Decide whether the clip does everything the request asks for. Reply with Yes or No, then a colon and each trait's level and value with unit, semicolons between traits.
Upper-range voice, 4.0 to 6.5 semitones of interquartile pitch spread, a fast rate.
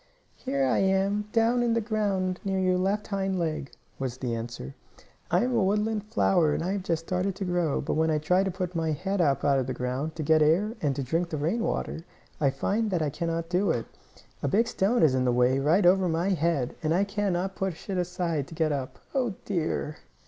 No: medium, 175 Hz; average, 4.4 semitones; fast, 225 wpm